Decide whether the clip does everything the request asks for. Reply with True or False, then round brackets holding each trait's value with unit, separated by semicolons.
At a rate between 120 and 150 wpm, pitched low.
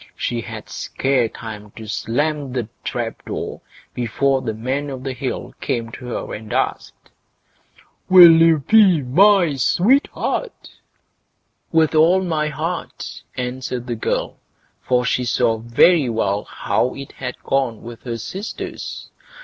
True (140 wpm; 130 Hz)